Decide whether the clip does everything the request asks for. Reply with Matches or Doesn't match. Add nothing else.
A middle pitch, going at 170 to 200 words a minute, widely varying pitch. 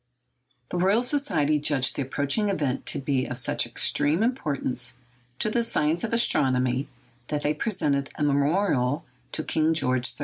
Doesn't match